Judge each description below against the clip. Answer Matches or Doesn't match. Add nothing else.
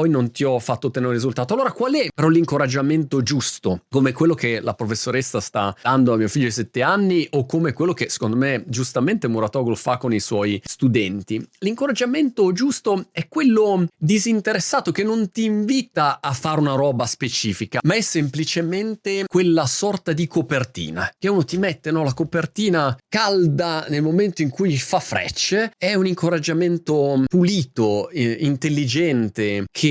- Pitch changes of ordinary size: Doesn't match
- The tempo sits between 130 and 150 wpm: Doesn't match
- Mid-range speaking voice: Matches